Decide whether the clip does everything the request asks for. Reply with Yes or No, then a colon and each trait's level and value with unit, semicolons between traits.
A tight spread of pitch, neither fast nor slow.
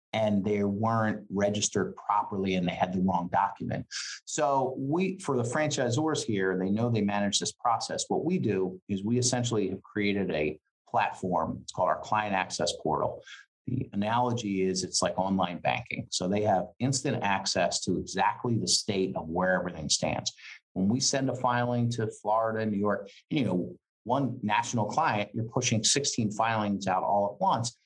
No: average, 4.0 semitones; average, 175 wpm